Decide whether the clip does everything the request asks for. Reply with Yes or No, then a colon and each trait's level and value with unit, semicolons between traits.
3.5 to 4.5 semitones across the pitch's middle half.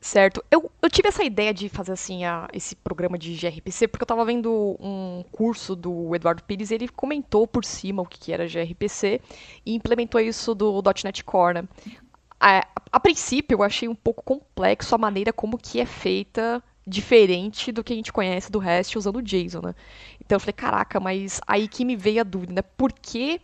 Yes: average, 3.8 semitones